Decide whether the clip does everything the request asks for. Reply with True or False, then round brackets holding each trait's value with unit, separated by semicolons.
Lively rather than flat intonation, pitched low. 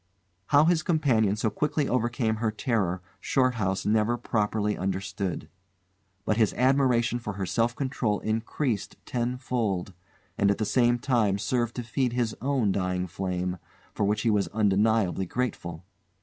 False (3.8 semitones; 110 Hz)